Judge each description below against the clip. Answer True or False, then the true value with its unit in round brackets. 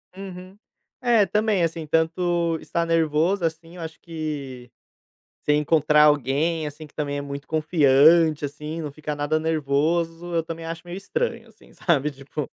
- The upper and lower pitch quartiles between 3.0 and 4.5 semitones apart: False (2.4 semitones)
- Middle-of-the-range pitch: True (160 Hz)